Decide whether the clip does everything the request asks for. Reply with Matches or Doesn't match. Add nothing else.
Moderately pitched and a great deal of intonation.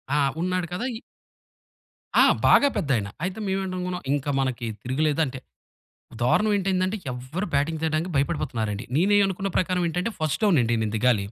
Matches